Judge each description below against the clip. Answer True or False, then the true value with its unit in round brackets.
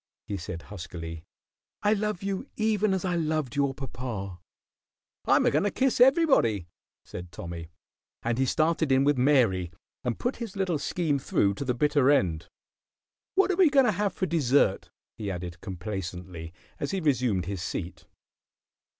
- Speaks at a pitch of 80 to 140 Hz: True (135 Hz)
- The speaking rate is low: False (165 wpm)